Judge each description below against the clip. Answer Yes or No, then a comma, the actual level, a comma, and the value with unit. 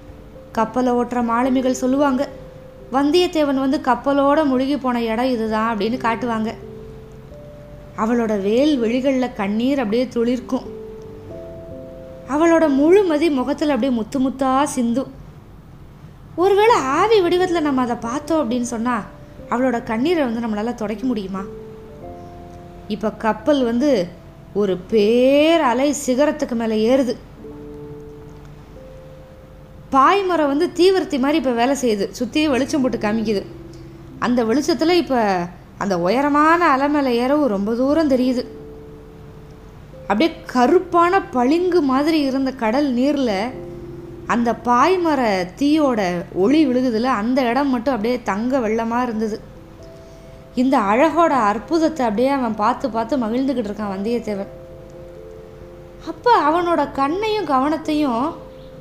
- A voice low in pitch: No, very high, 250 Hz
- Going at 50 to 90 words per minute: No, average, 105 wpm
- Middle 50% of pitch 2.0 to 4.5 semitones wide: No, average, 5.1 semitones